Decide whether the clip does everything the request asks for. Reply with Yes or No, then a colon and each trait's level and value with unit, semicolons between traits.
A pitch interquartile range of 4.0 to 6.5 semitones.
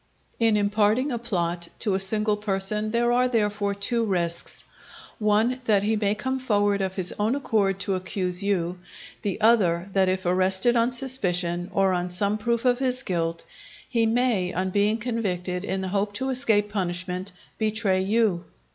No: average, 3.5 semitones